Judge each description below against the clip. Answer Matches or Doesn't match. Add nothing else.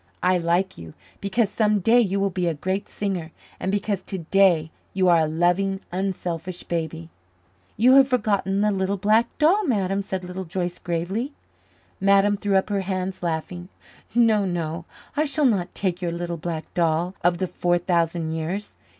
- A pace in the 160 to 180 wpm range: Matches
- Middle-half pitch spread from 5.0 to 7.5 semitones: Doesn't match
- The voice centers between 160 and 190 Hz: Matches